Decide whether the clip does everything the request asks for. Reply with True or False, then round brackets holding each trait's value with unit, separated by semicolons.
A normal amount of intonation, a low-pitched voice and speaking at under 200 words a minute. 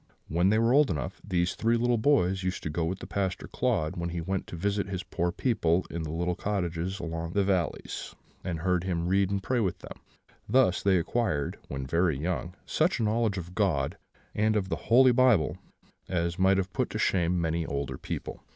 False (3.5 semitones; 90 Hz; 205 wpm)